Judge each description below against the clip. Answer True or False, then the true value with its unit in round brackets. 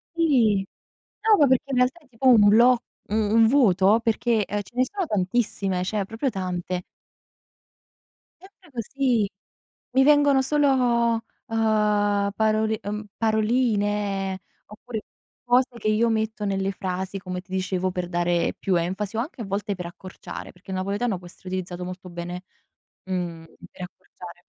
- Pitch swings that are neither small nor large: True (4.5 semitones)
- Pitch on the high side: True (210 Hz)